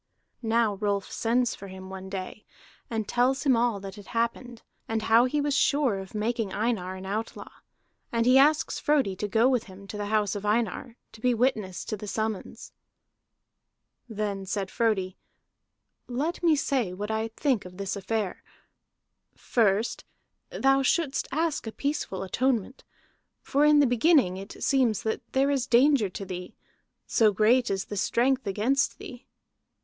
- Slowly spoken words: No, average, 165 wpm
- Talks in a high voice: Yes, high, 225 Hz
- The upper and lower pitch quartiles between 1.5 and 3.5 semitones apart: No, average, 4.5 semitones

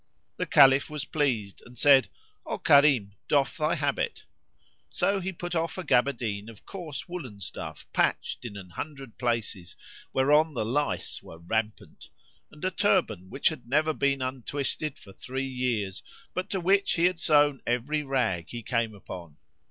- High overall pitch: No, low, 135 Hz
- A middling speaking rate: Yes, average, 160 wpm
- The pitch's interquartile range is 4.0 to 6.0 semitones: Yes, wide, 5.5 semitones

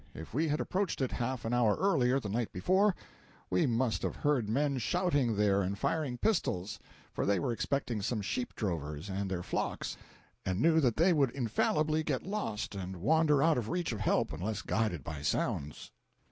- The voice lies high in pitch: No, low, 120 Hz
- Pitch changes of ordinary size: No, wide, 7.0 semitones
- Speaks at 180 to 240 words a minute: Yes, average, 190 wpm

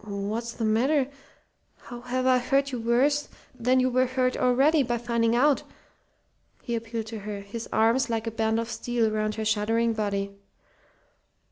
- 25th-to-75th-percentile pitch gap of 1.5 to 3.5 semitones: Yes, narrow, 2.5 semitones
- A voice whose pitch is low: No, high, 235 Hz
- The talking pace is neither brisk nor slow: Yes, average, 165 wpm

